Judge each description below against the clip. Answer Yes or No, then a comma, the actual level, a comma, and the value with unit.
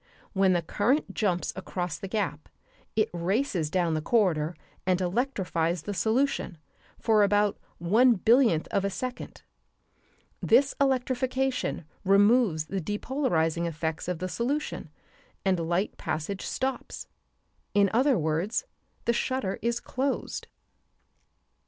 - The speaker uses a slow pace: Yes, slow, 120 wpm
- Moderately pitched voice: No, high, 200 Hz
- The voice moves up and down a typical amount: No, wide, 6.1 semitones